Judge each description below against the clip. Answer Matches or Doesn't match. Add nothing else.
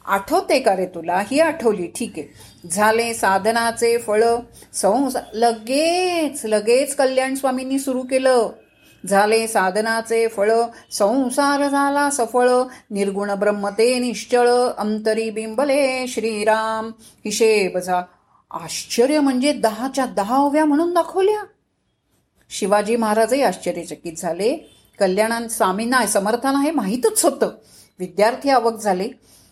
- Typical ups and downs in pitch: Matches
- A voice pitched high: Matches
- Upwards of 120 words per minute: Doesn't match